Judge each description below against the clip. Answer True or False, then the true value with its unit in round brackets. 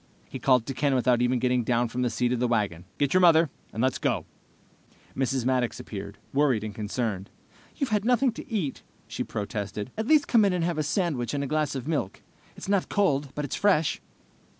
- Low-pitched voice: True (130 Hz)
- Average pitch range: False (5.8 semitones)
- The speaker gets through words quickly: True (215 wpm)